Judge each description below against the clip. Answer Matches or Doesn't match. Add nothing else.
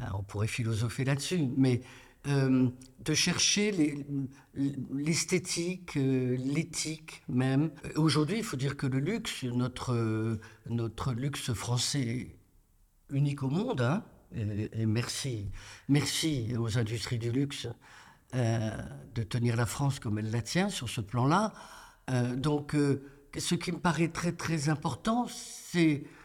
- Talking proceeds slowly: Matches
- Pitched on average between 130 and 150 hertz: Matches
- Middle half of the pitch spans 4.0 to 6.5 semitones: Matches